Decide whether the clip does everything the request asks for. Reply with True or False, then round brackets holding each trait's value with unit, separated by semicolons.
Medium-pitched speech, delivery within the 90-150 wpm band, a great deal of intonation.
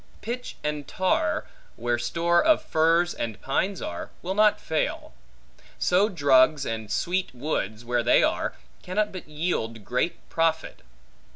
True (155 Hz; 135 wpm; 6.9 semitones)